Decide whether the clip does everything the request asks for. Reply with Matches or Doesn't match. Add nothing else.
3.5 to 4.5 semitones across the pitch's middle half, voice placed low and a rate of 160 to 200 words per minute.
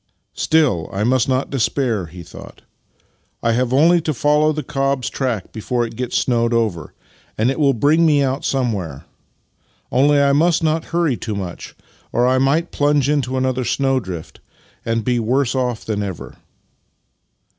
Matches